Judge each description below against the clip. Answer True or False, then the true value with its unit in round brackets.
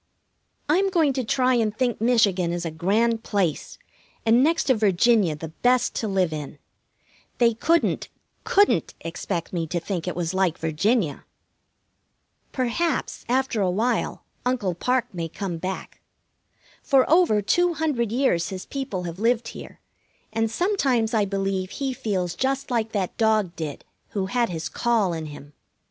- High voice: True (215 Hz)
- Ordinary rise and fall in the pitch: False (5.9 semitones)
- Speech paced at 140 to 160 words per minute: True (155 wpm)